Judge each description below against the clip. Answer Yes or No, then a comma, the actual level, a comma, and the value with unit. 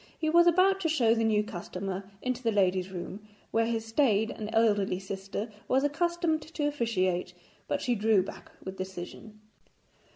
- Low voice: No, high, 225 Hz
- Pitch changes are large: Yes, wide, 6.9 semitones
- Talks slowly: No, average, 165 wpm